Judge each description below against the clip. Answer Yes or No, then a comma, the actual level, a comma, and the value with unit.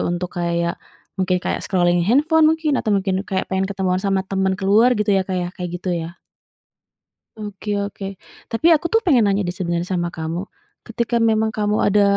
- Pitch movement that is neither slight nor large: Yes, average, 3.1 semitones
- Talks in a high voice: Yes, high, 195 Hz